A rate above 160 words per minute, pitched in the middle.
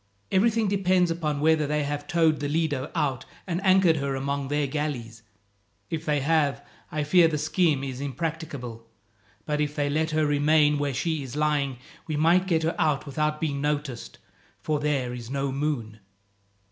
Yes: average, 170 wpm; medium, 150 Hz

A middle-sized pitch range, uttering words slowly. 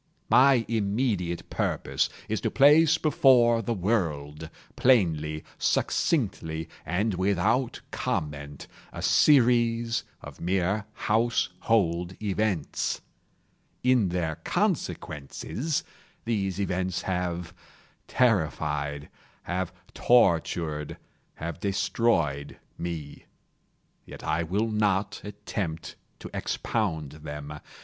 No: wide, 6.2 semitones; slow, 80 wpm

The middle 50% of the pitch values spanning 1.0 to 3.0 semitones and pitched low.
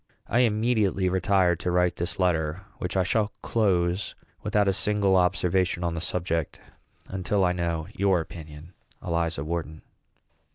Yes: narrow, 2.6 semitones; very low, 90 Hz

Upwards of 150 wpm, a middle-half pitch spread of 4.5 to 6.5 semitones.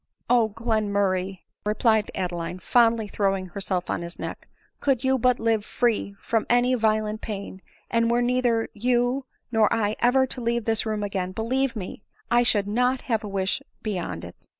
No: average, 180 wpm; average, 3.3 semitones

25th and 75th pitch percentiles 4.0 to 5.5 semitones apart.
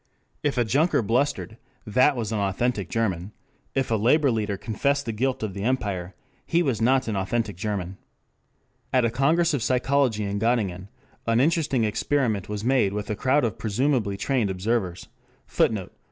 Yes: average, 4.5 semitones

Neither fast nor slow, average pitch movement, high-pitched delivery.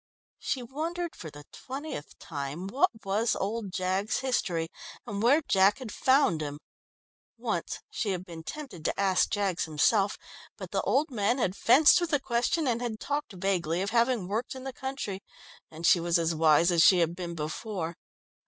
No: average, 180 wpm; wide, 7.1 semitones; high, 200 Hz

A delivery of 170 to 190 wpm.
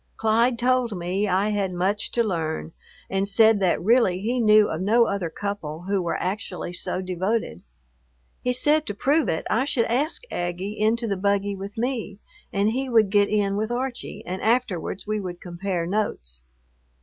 Yes: average, 175 wpm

